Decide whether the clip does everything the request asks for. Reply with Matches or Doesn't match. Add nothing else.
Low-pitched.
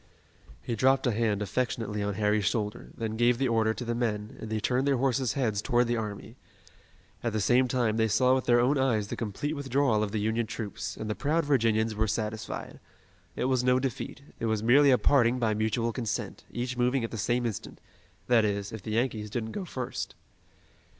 Matches